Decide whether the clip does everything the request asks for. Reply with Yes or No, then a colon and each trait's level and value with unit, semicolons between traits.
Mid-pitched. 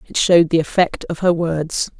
Yes: medium, 165 Hz